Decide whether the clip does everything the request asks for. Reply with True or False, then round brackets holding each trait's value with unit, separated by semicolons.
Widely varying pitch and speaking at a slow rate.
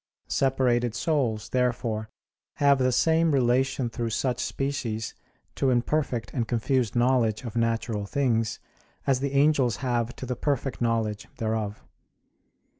False (2.8 semitones; 125 wpm)